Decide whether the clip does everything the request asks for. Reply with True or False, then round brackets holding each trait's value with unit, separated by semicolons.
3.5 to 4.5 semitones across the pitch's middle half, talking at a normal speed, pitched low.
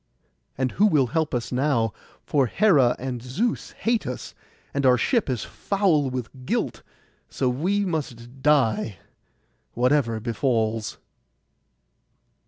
False (4.2 semitones; 120 wpm; 130 Hz)